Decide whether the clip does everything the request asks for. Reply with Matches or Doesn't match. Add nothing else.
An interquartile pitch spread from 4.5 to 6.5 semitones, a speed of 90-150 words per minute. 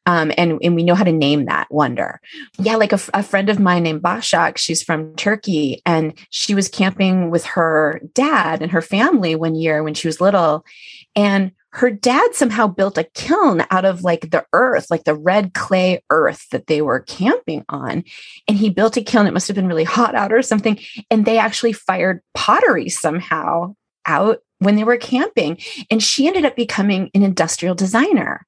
Doesn't match